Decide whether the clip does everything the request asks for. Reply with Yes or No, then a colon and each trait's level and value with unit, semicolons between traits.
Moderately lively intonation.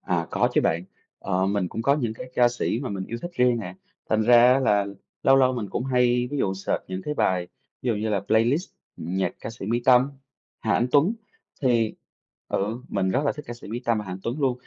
Yes: average, 3.9 semitones